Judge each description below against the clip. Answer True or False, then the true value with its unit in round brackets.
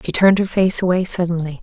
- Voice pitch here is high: False (175 Hz)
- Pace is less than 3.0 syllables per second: False (6.5 syllables/s)